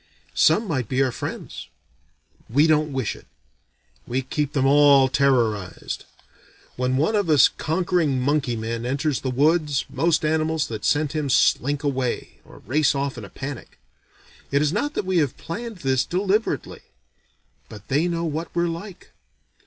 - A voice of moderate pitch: Yes, medium, 145 Hz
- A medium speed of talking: Yes, average, 160 wpm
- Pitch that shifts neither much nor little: Yes, average, 3.8 semitones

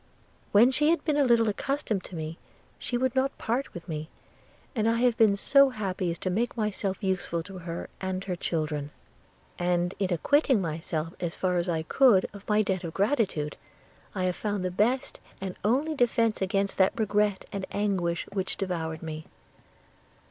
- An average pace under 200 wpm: Yes, average, 175 wpm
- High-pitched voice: Yes, high, 195 Hz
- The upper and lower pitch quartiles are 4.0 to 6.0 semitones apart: Yes, average, 4.6 semitones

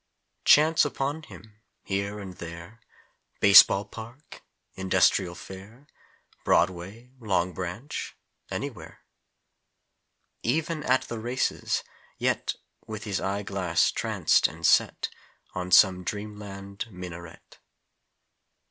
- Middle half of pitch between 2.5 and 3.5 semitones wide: No, average, 4.1 semitones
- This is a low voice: Yes, low, 100 Hz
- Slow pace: Yes, slow, 105 wpm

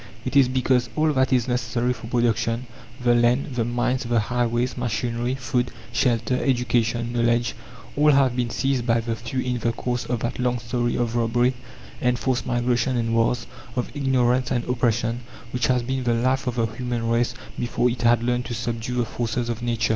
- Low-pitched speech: Yes, low, 120 Hz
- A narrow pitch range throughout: Yes, narrow, 1.2 semitones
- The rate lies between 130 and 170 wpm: No, average, 190 wpm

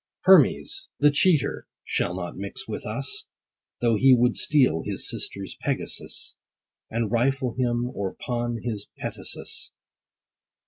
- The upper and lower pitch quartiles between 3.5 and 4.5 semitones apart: Yes, average, 3.9 semitones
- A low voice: Yes, low, 120 Hz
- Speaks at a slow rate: Yes, slow, 125 wpm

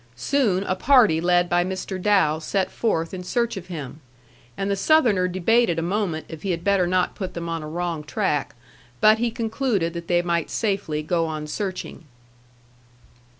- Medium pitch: Yes, medium, 180 Hz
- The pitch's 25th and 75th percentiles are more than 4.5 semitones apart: No, average, 3.6 semitones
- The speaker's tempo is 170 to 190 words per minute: Yes, average, 180 wpm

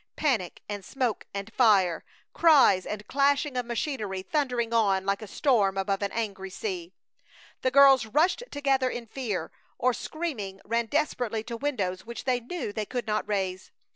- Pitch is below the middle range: No, high, 230 Hz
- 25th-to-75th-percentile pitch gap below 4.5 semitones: No, average, 5.3 semitones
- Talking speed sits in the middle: Yes, average, 165 wpm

